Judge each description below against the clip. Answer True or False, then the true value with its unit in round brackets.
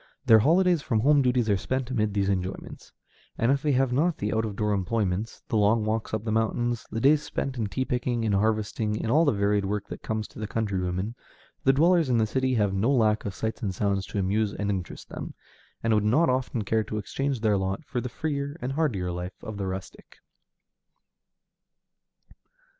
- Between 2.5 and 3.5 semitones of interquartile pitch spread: False (4.2 semitones)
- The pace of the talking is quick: True (210 wpm)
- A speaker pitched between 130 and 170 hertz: False (110 Hz)